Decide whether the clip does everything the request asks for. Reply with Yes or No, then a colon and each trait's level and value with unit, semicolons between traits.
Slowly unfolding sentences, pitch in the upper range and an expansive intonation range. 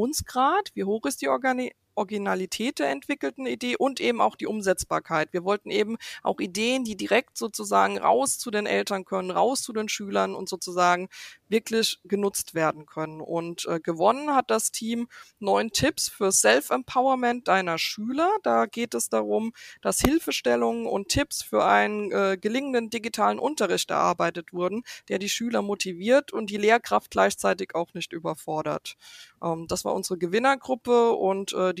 No: average, 160 wpm; high, 200 Hz; wide, 6.1 semitones